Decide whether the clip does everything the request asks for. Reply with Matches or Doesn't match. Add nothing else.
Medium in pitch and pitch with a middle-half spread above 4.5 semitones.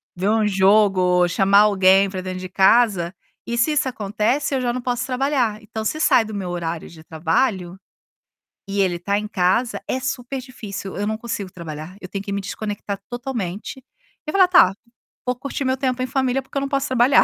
Doesn't match